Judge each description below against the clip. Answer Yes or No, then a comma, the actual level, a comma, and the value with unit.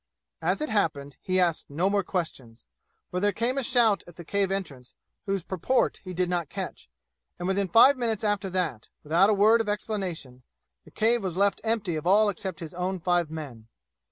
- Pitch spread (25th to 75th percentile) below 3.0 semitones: No, average, 3.9 semitones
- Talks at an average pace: Yes, average, 195 wpm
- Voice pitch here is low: No, medium, 185 Hz